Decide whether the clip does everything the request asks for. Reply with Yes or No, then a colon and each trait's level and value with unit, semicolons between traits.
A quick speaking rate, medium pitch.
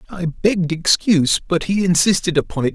No: average, 175 wpm; medium, 175 Hz